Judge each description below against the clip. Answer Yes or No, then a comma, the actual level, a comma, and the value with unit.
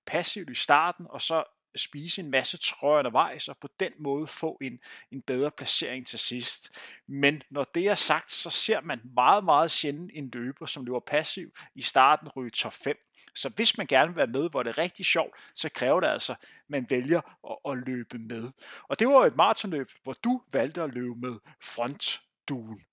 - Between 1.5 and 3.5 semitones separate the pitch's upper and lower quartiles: No, average, 4.0 semitones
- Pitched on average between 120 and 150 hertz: Yes, medium, 140 Hz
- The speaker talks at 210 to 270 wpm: No, average, 200 wpm